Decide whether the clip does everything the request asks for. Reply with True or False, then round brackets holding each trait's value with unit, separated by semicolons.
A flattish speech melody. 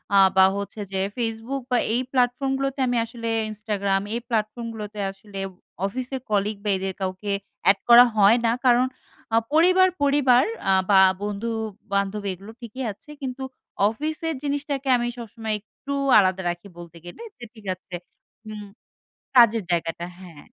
False (4.0 semitones)